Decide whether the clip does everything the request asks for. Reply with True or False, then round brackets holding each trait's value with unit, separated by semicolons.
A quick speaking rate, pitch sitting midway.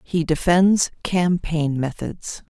False (95 wpm; 165 Hz)